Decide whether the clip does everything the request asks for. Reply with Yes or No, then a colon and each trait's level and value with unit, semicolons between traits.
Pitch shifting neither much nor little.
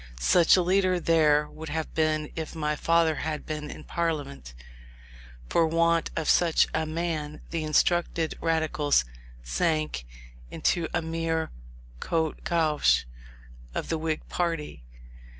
No: narrow, 1.6 semitones